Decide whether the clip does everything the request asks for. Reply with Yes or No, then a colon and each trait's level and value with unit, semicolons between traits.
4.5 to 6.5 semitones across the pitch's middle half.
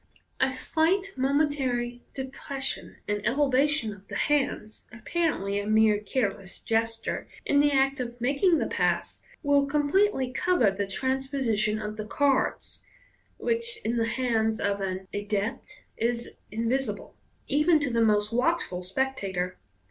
Yes: average, 5.0 semitones